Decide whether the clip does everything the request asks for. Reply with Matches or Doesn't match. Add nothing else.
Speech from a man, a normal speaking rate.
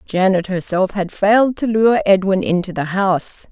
Doesn't match